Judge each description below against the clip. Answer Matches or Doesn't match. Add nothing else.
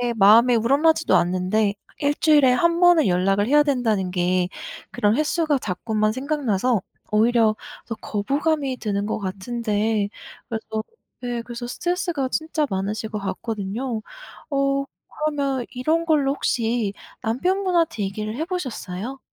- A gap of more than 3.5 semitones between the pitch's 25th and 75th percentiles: Matches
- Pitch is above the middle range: Matches